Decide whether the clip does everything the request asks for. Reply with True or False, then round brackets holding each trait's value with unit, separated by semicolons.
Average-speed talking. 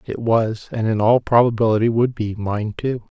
True (190 wpm)